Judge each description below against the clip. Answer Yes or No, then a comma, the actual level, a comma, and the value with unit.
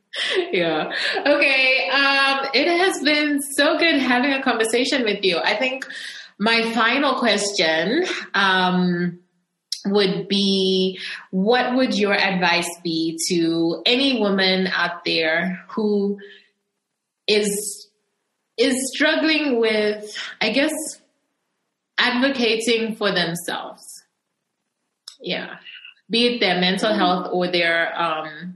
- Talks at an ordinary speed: No, slow, 105 wpm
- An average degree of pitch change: No, wide, 6.4 semitones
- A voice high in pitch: Yes, high, 210 Hz